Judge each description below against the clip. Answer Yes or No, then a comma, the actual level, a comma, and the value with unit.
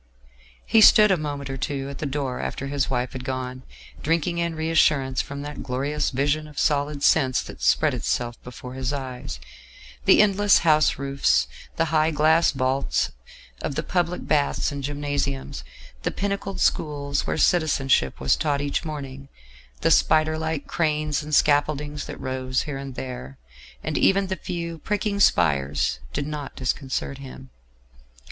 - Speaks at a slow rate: No, average, 155 wpm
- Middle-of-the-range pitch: Yes, medium, 145 Hz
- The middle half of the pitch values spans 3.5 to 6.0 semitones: No, average, 3.0 semitones